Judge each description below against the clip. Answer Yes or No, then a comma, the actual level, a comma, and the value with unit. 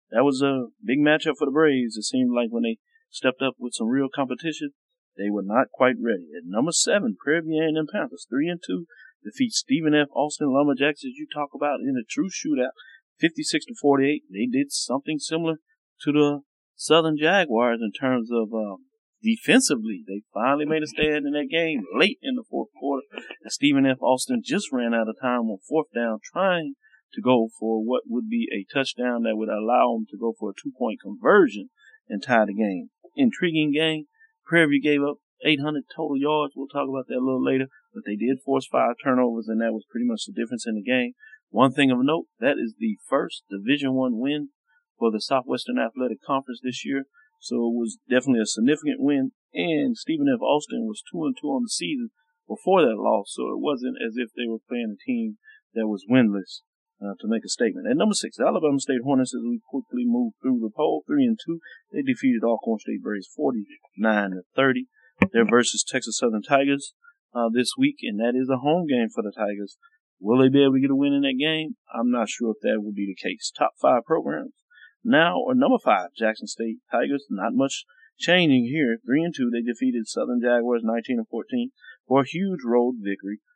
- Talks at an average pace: No, fast, 210 wpm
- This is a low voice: No, medium, 150 Hz